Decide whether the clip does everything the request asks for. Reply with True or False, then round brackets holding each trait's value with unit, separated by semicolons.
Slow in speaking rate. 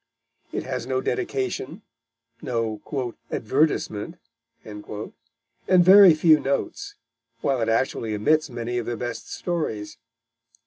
True (105 wpm)